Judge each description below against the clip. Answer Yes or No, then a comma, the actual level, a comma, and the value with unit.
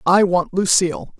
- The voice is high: No, medium, 180 Hz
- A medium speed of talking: Yes, average, 150 wpm